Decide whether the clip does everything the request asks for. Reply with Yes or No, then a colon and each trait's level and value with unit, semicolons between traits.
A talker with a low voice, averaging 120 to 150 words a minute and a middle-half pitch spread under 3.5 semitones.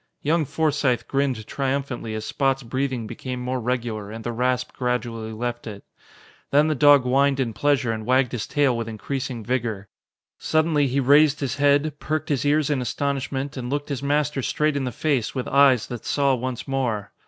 No: low, 130 Hz; average, 185 wpm; average, 2.9 semitones